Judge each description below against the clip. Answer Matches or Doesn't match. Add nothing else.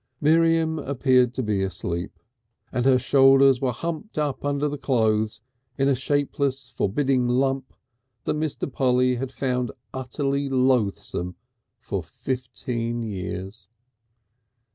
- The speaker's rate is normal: Doesn't match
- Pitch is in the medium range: Doesn't match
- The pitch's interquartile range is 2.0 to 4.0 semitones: Matches